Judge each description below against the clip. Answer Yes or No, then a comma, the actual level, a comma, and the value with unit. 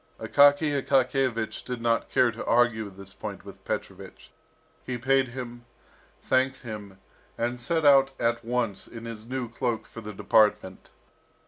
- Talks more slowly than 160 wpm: Yes, average, 145 wpm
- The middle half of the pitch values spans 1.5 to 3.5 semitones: Yes, average, 2.7 semitones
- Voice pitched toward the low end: Yes, low, 120 Hz